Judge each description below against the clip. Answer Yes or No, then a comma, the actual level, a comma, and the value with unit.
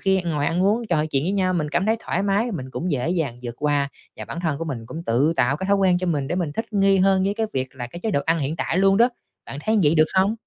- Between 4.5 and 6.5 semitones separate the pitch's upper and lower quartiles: Yes, average, 5.1 semitones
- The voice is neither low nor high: Yes, medium, 170 Hz